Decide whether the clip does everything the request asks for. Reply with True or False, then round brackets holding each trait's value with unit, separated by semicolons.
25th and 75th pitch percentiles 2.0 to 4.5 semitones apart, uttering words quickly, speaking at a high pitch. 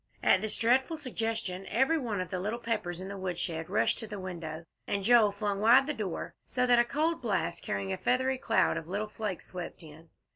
False (5.0 semitones; 215 wpm; 210 Hz)